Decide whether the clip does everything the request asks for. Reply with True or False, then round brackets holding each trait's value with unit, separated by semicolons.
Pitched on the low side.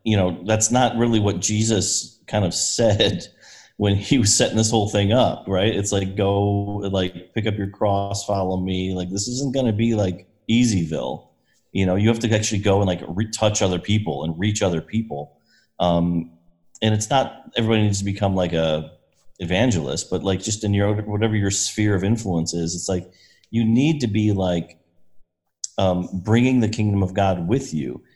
True (100 Hz)